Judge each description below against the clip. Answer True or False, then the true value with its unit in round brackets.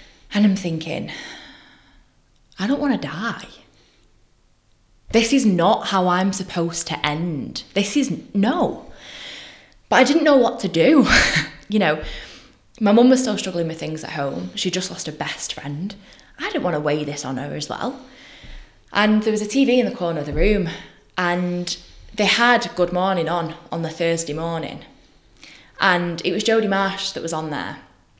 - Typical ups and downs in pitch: True (4.5 semitones)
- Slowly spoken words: False (175 wpm)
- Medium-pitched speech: True (180 Hz)